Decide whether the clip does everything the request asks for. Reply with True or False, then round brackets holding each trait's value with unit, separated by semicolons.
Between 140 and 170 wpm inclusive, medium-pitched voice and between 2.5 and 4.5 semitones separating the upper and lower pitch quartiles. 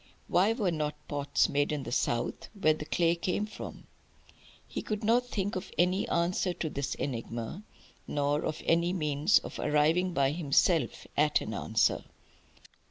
True (160 wpm; 160 Hz; 4.0 semitones)